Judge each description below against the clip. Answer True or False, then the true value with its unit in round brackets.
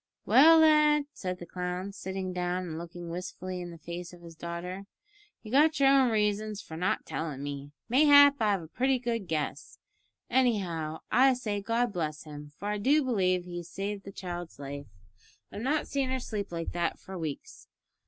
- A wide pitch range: True (6.1 semitones)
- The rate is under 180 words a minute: False (185 wpm)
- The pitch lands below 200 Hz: True (185 Hz)